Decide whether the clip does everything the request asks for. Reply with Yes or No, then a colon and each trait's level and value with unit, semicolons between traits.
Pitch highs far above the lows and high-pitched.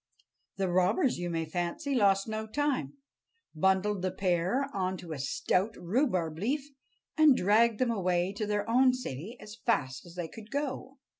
Yes: wide, 5.7 semitones; high, 205 Hz